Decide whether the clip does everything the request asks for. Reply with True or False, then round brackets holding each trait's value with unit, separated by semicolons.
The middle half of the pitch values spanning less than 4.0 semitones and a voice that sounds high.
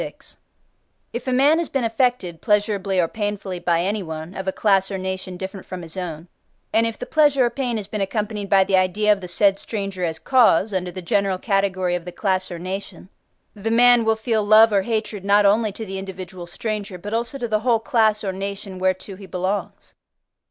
True (2.9 semitones; 200 Hz)